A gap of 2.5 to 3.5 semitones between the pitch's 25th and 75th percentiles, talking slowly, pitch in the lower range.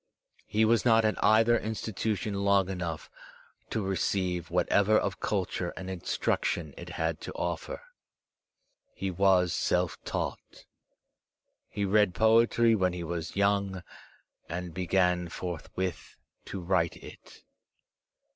Yes: average, 2.9 semitones; slow, 120 wpm; very low, 95 Hz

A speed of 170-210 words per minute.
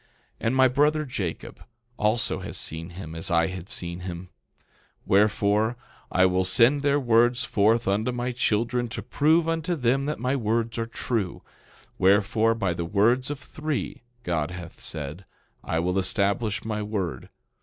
No: average, 160 wpm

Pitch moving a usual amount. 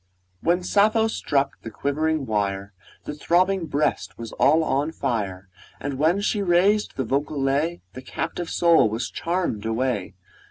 No: wide, 6.6 semitones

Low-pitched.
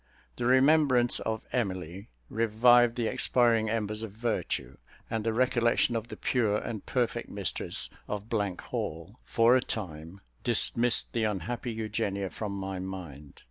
Yes: low, 110 Hz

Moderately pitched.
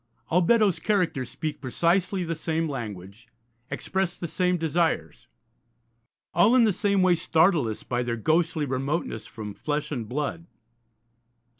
Yes: medium, 160 Hz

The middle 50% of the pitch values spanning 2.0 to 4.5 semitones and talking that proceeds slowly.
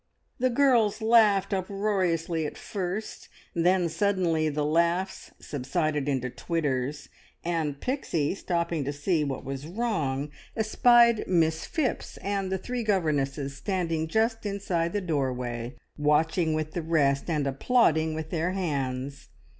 No: average, 5.2 semitones; slow, 130 wpm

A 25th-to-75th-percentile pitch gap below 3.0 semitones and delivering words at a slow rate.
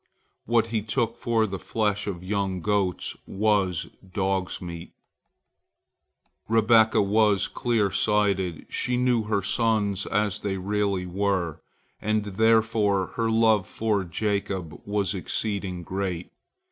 Yes: narrow, 2.5 semitones; slow, 120 wpm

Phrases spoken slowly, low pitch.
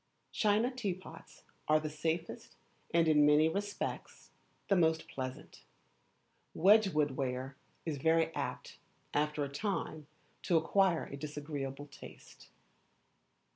No: slow, 110 wpm; medium, 155 Hz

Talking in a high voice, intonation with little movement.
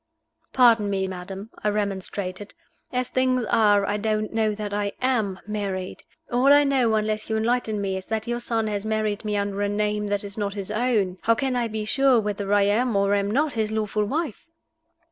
Yes: high, 210 Hz; narrow, 2.2 semitones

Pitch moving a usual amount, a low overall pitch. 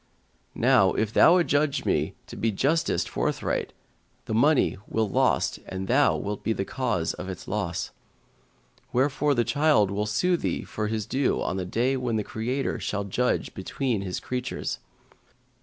Yes: average, 4.9 semitones; low, 115 Hz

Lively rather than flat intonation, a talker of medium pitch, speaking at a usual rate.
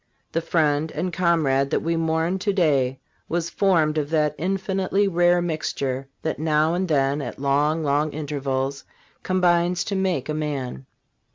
No: average, 3.4 semitones; medium, 155 Hz; average, 155 wpm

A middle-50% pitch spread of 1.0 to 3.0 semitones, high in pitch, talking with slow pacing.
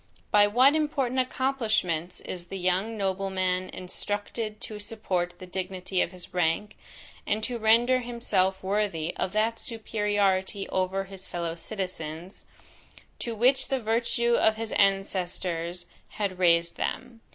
No: average, 3.6 semitones; high, 195 Hz; slow, 130 wpm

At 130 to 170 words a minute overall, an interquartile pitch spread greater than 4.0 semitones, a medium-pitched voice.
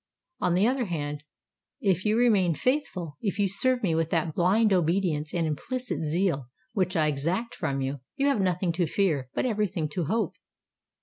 No: average, 180 wpm; average, 5.1 semitones; medium, 180 Hz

